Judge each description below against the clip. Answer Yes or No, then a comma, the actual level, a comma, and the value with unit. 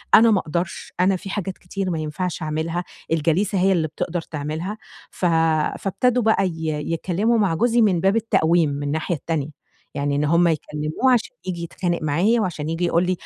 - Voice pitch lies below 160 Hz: No, medium, 175 Hz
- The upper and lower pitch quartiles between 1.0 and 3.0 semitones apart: No, average, 3.6 semitones